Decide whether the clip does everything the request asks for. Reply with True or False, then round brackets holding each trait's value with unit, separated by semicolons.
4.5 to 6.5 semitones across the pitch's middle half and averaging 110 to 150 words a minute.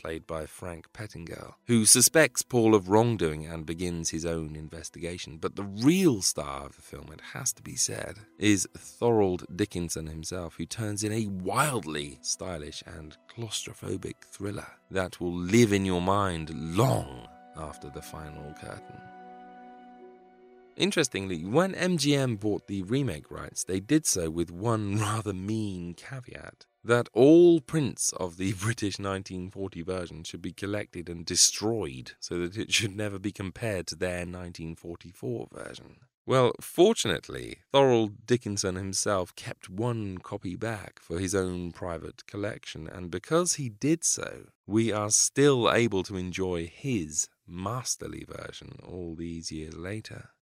True (5.3 semitones; 145 wpm)